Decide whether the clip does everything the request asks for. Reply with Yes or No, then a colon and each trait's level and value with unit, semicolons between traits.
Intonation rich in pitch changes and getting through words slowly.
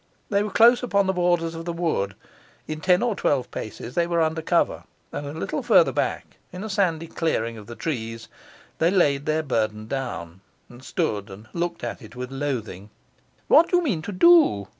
No: wide, 7.4 semitones; average, 200 wpm